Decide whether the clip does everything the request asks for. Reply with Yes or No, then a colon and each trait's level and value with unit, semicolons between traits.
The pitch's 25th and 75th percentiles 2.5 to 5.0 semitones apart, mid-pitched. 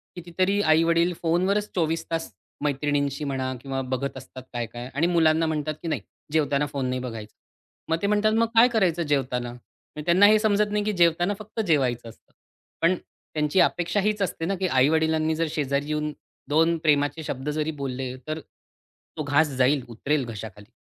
Yes: average, 4.3 semitones; medium, 155 Hz